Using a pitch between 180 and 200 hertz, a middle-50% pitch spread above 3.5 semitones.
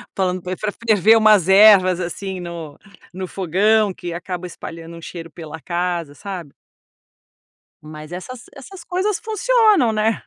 Yes: medium, 185 Hz; average, 4.0 semitones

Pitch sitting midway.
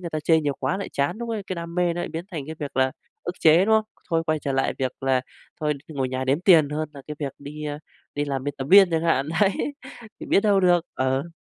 Yes: medium, 155 Hz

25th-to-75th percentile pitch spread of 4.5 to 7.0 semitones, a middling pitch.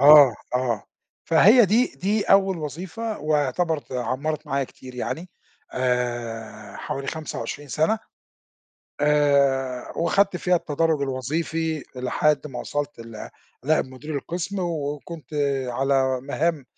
No: average, 4.1 semitones; medium, 145 Hz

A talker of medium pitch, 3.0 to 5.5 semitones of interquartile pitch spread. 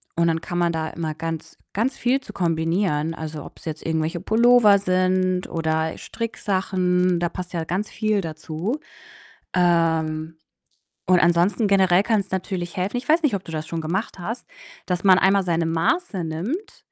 Yes: medium, 180 Hz; average, 3.5 semitones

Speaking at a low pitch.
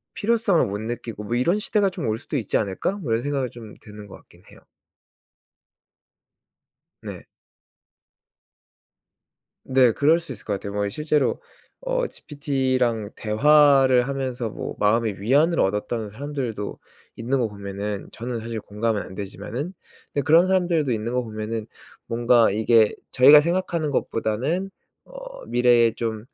Yes: low, 120 Hz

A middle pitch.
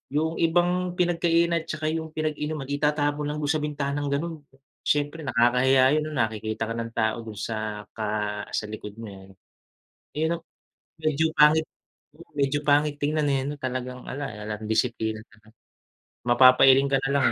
Yes: medium, 145 Hz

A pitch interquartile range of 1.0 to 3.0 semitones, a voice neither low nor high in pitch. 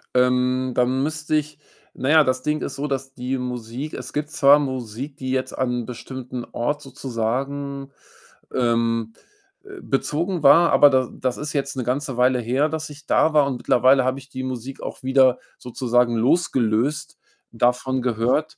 No: narrow, 2.4 semitones; low, 130 Hz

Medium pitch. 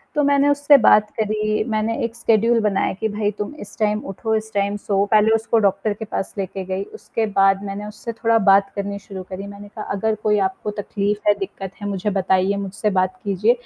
No: high, 205 Hz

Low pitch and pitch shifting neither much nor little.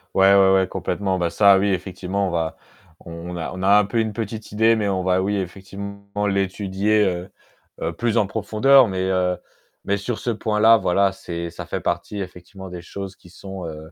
No: very low, 95 Hz; narrow, 2.2 semitones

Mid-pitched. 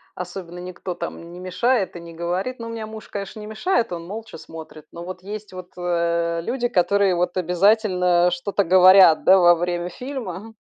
Yes: medium, 180 Hz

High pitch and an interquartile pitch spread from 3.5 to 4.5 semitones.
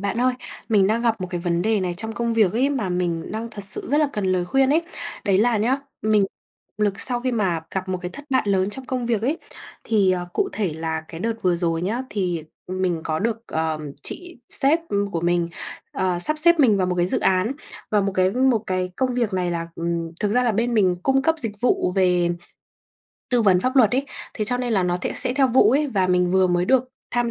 No: high, 205 Hz; average, 5.2 semitones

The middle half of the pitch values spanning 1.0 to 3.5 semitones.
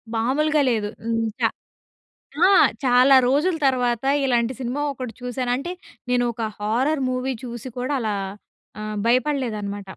Yes: average, 2.7 semitones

